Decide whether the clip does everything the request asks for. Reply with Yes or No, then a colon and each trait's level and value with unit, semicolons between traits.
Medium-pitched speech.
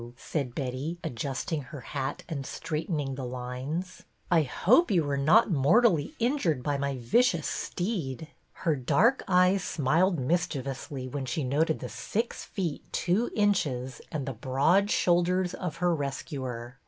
Yes: medium, 150 Hz